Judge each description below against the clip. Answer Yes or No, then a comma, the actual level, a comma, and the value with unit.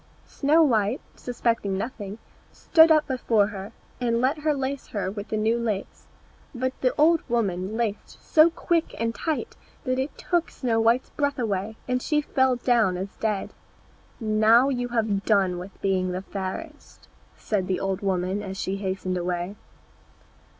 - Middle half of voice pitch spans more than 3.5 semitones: Yes, average, 5.0 semitones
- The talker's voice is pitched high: Yes, high, 225 Hz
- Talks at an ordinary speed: Yes, average, 160 wpm